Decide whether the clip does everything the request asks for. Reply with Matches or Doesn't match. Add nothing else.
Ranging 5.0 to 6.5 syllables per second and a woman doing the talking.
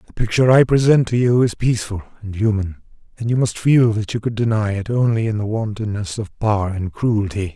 Doesn't match